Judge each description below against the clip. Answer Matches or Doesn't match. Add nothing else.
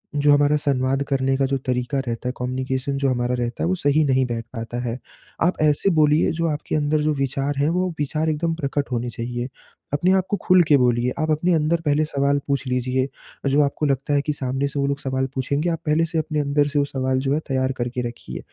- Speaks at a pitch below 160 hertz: Matches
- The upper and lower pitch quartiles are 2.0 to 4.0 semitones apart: Matches